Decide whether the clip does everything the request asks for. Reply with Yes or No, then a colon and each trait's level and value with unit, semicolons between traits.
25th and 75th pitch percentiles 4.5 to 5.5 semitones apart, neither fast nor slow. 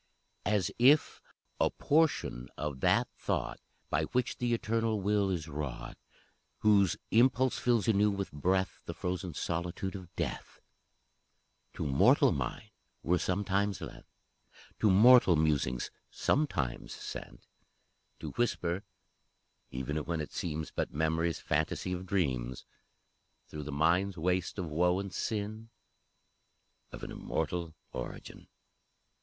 No: average, 5.2 semitones; slow, 120 wpm